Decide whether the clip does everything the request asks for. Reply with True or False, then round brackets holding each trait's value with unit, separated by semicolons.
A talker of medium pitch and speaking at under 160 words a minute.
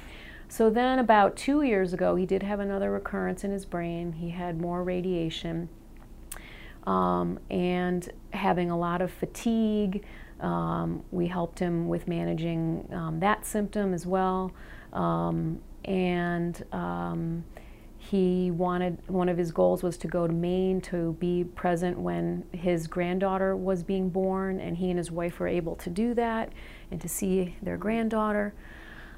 True (180 Hz; 150 wpm)